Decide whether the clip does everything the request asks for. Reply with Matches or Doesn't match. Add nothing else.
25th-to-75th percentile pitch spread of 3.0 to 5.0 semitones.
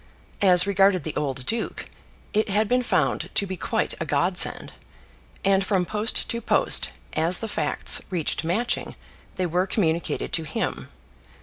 Matches